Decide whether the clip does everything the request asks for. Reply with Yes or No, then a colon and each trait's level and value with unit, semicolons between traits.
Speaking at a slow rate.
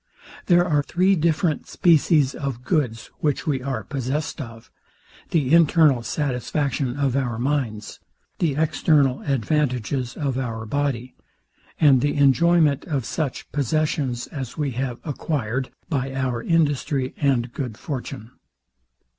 Yes: slow, 120 wpm